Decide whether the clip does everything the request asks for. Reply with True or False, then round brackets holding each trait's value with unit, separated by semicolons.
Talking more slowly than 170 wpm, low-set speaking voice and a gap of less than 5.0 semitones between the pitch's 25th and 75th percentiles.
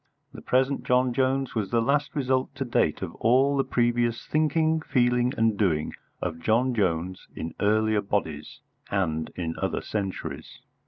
False (155 wpm; 120 Hz; 5.5 semitones)